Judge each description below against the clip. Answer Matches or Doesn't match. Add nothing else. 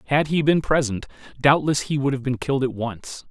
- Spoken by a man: Matches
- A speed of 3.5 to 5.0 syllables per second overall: Doesn't match